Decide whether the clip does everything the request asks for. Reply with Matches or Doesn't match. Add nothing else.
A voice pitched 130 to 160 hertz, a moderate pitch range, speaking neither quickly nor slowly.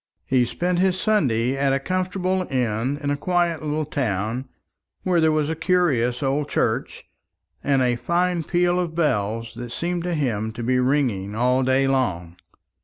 Doesn't match